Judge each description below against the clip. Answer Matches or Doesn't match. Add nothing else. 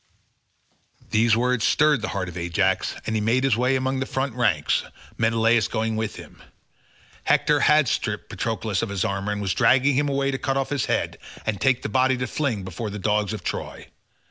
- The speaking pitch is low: Matches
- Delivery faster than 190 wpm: Matches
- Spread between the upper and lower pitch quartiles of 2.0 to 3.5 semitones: Doesn't match